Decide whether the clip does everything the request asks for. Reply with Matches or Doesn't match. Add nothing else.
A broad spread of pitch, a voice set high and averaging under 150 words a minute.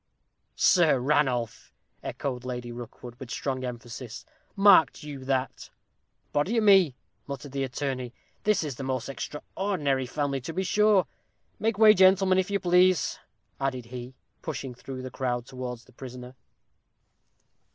Doesn't match